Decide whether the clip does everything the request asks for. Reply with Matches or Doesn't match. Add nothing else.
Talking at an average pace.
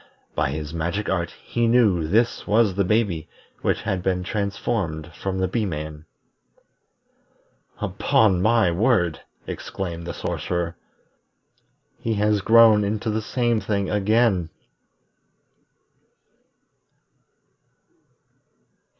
Doesn't match